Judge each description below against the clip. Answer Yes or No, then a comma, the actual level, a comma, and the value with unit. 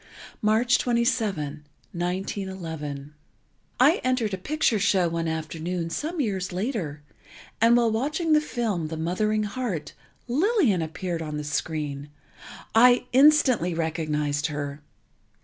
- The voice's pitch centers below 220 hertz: Yes, high, 190 Hz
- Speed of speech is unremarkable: No, slow, 115 wpm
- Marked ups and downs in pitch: Yes, wide, 7.1 semitones